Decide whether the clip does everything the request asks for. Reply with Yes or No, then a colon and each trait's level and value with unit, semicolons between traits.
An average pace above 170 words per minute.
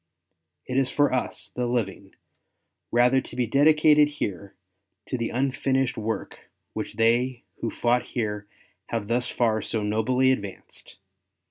No: slow, 135 wpm